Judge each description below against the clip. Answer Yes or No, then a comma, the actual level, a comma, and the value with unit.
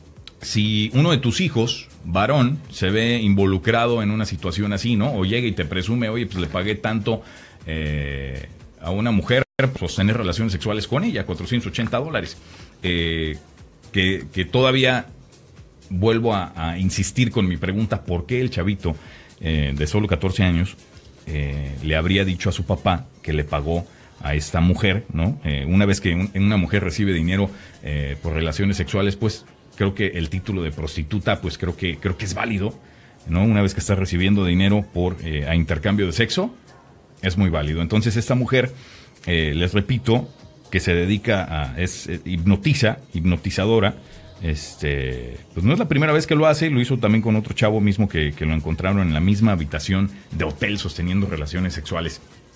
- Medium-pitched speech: No, very low, 95 Hz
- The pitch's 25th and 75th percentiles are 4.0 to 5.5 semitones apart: Yes, average, 4.4 semitones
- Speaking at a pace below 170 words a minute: No, average, 180 wpm